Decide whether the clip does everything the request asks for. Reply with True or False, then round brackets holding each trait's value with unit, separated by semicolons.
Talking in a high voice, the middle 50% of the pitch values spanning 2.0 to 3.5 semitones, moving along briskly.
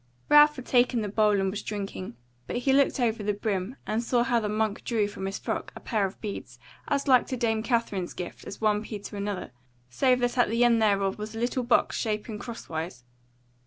True (220 Hz; 3.1 semitones; 220 wpm)